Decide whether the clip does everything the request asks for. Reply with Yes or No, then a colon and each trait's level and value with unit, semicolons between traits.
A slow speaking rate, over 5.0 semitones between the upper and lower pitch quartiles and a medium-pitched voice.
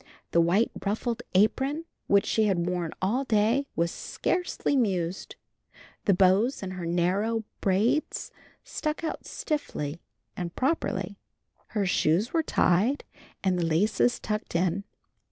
No: slow, 130 wpm; wide, 5.4 semitones; high, 200 Hz